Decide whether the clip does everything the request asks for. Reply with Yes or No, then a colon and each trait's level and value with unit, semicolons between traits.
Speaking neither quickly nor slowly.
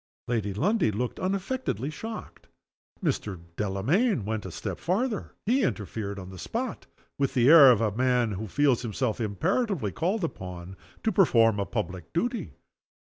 Yes: average, 155 wpm